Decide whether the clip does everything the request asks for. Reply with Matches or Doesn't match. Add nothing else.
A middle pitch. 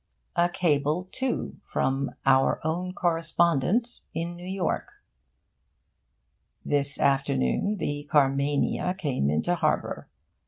Matches